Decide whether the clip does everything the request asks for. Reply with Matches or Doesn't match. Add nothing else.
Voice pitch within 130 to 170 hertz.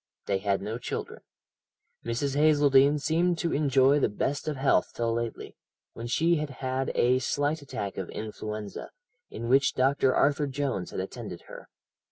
Matches